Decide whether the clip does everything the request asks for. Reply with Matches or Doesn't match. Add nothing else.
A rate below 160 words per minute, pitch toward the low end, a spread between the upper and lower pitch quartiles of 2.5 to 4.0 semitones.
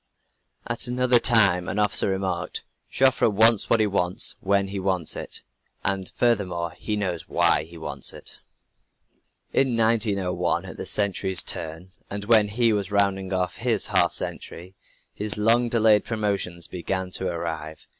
Matches